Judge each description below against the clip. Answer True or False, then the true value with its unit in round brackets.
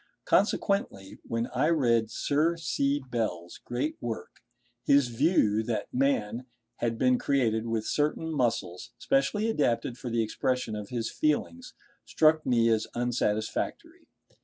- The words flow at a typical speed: False (130 wpm)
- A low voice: True (120 Hz)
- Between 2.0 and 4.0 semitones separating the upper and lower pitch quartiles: False (4.5 semitones)